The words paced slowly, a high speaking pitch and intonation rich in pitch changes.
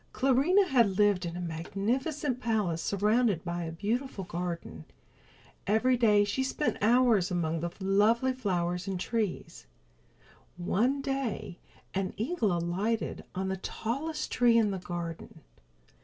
Yes: slow, 130 wpm; high, 205 Hz; wide, 5.7 semitones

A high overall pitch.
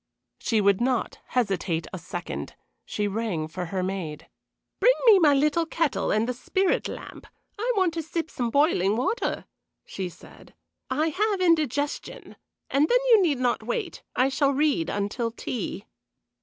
Yes: very high, 255 Hz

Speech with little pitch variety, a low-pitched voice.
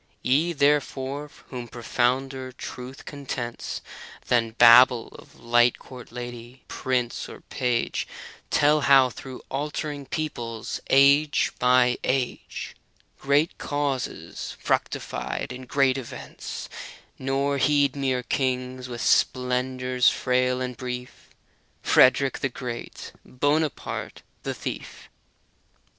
Yes: narrow, 1.9 semitones; low, 130 Hz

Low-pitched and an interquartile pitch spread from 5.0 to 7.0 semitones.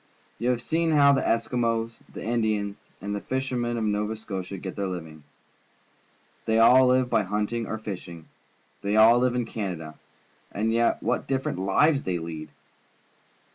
No: low, 110 Hz; average, 3.7 semitones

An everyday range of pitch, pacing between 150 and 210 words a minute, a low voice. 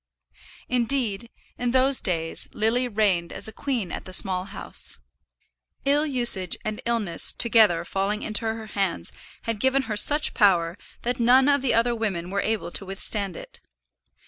No: average, 4.2 semitones; average, 160 wpm; high, 220 Hz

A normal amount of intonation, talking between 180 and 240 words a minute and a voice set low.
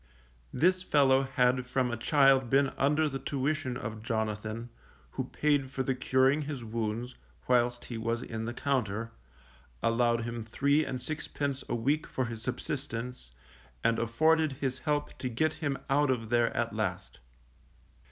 No: average, 3.4 semitones; average, 155 wpm; low, 125 Hz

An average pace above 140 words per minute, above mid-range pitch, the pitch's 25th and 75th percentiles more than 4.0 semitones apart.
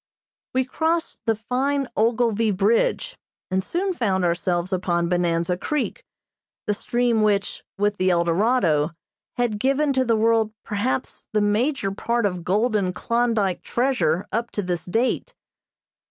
No: slow, 135 wpm; high, 215 Hz; average, 4.9 semitones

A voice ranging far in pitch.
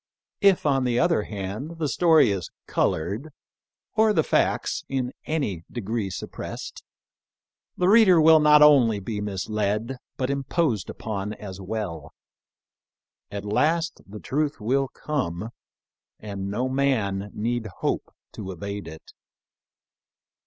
Yes: wide, 6.7 semitones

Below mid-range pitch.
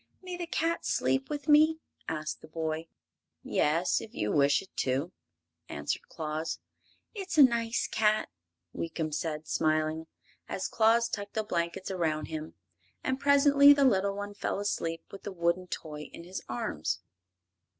No: medium, 185 Hz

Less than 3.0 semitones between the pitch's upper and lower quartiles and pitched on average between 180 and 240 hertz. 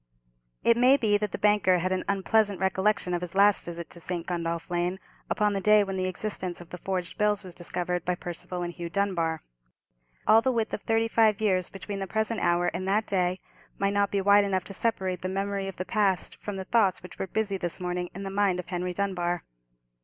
Yes: narrow, 2.5 semitones; high, 190 Hz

